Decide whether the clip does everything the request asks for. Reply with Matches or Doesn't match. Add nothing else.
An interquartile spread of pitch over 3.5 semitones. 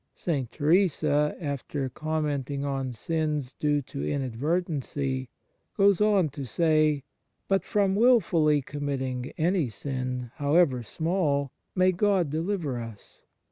Matches